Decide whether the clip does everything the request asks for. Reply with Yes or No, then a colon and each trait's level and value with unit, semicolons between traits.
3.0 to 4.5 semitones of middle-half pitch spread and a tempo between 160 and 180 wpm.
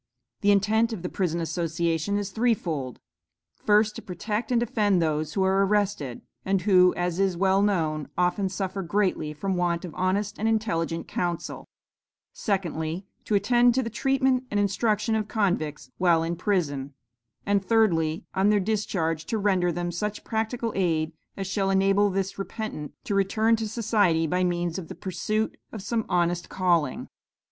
Yes: average, 3.6 semitones; average, 165 wpm